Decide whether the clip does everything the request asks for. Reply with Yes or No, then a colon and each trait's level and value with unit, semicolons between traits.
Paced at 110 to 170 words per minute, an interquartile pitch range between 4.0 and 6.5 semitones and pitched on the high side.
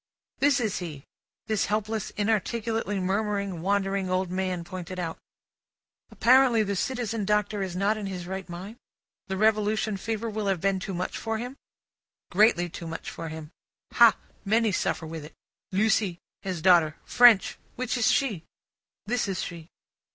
No: average, 155 wpm; average, 3.3 semitones; high, 200 Hz